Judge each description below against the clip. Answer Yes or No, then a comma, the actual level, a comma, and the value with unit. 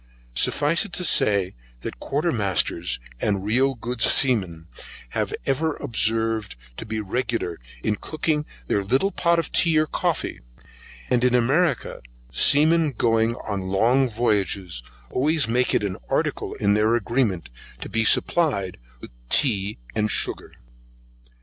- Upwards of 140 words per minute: No, slow, 135 wpm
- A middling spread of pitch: No, wide, 5.7 semitones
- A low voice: Yes, low, 115 Hz